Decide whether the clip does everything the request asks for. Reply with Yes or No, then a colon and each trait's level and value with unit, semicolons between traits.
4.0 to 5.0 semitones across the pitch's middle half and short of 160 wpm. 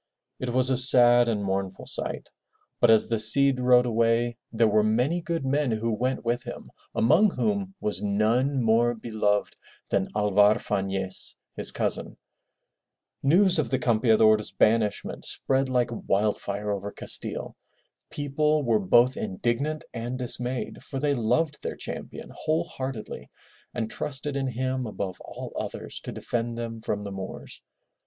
No: average, 3.6 semitones; average, 150 wpm